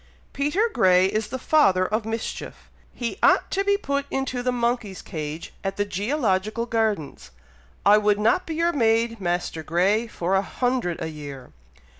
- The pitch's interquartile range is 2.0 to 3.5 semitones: No, average, 5.2 semitones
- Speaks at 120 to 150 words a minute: No, average, 165 wpm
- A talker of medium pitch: No, high, 215 Hz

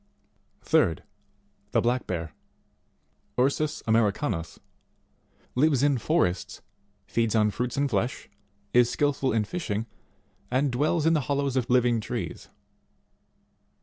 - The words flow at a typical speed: No, slow, 115 wpm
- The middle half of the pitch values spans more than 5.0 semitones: No, average, 4.3 semitones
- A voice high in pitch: No, low, 125 Hz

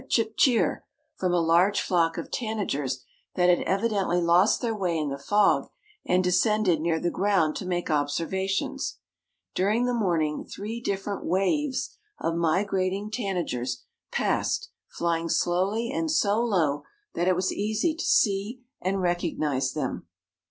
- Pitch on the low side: No, medium, 185 Hz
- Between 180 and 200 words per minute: No, average, 145 wpm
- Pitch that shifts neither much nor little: Yes, average, 3.9 semitones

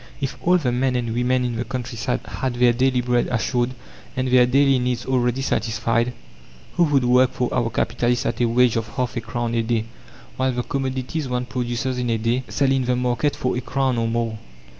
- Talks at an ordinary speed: No, fast, 210 wpm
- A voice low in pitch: Yes, low, 125 Hz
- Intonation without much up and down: Yes, narrow, 1.4 semitones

